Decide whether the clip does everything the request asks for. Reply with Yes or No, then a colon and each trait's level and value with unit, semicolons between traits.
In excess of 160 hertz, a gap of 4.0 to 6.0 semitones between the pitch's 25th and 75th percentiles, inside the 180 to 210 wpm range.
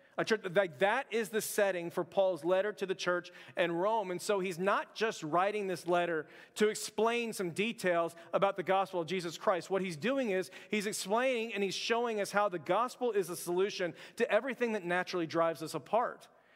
No: high, 190 Hz; average, 3.3 semitones; average, 200 wpm